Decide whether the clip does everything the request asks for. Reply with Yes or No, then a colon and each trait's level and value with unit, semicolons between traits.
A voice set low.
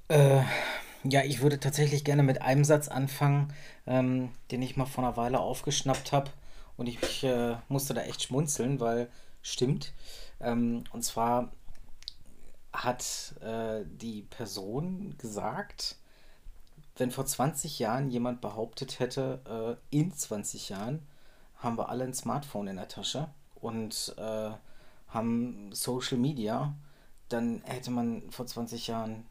Yes: low, 125 Hz